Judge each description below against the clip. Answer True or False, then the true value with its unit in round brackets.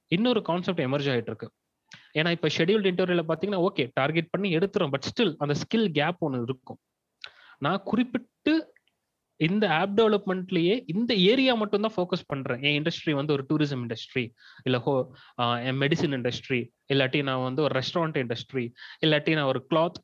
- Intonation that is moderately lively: False (6.0 semitones)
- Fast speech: True (150 wpm)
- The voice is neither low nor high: True (155 Hz)